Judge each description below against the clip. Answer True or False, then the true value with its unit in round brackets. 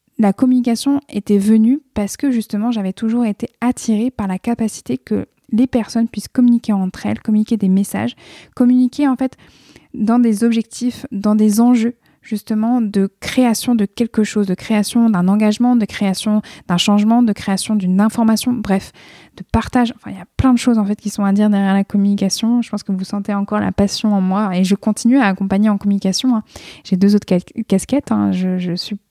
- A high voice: True (215 Hz)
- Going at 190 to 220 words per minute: True (200 wpm)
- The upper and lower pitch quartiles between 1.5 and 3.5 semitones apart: True (2.9 semitones)